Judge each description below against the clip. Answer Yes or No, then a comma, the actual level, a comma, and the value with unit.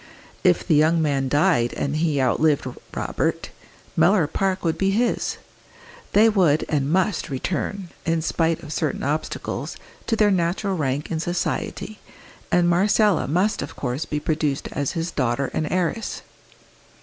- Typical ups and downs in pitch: Yes, average, 4.3 semitones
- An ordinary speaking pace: Yes, average, 150 wpm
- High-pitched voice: No, medium, 165 Hz